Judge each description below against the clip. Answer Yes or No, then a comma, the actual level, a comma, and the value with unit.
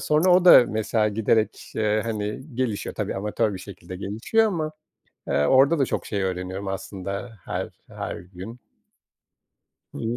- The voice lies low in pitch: Yes, low, 105 Hz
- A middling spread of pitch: Yes, average, 4.3 semitones